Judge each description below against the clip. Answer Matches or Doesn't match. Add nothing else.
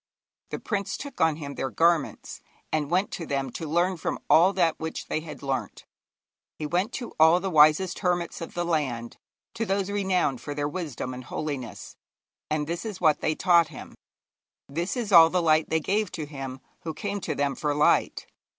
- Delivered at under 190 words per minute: Doesn't match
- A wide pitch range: Doesn't match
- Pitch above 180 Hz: Doesn't match